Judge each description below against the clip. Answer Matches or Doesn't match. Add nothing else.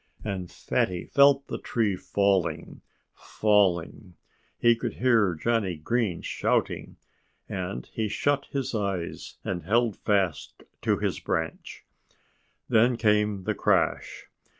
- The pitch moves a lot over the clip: Doesn't match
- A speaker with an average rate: Doesn't match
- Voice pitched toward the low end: Matches